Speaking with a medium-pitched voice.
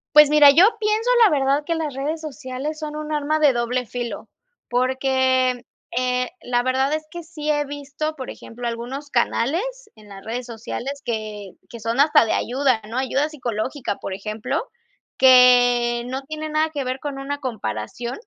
No: very high, 265 Hz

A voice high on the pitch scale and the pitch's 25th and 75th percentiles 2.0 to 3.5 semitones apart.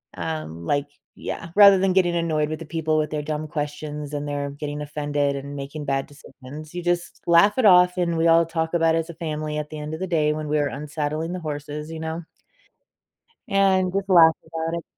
No: medium, 155 Hz; narrow, 2.5 semitones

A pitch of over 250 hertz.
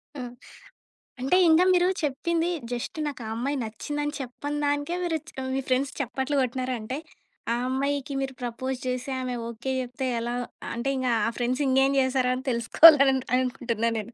Yes: very high, 260 Hz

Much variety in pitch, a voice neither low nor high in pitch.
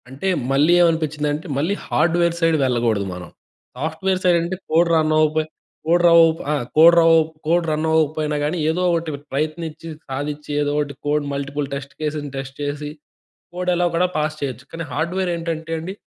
No: narrow, 2.4 semitones; medium, 155 Hz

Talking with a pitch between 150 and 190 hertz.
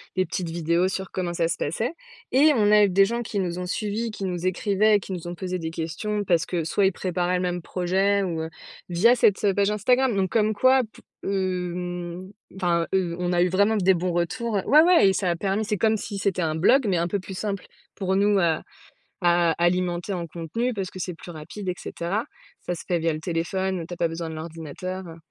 Yes: medium, 185 Hz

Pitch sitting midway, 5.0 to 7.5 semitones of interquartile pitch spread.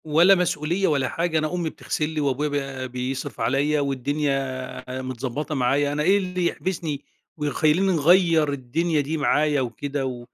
No: medium, 150 Hz; average, 3.0 semitones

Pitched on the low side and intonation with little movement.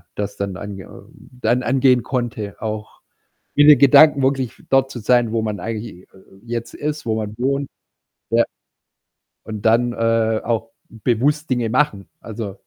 No: low, 115 Hz; average, 3.4 semitones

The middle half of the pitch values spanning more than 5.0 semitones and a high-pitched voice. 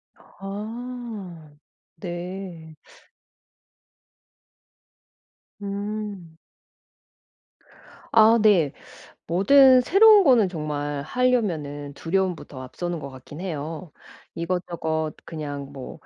No: wide, 5.6 semitones; medium, 175 Hz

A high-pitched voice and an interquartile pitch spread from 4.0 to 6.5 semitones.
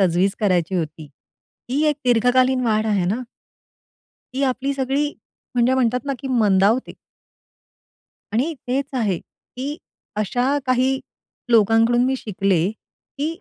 Yes: high, 245 Hz; average, 4.5 semitones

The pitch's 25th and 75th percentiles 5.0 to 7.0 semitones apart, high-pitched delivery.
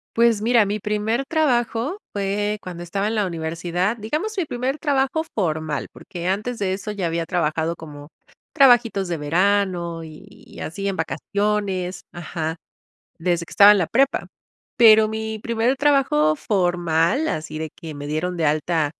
Yes: average, 5.3 semitones; high, 195 Hz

